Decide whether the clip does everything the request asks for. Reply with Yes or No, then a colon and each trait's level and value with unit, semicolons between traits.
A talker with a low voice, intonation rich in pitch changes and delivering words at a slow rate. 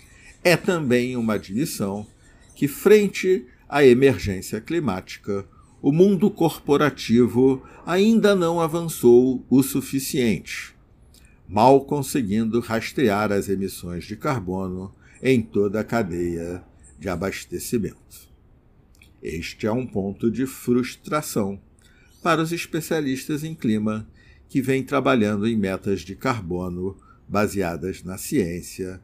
Yes: low, 115 Hz; wide, 6.6 semitones; slow, 105 wpm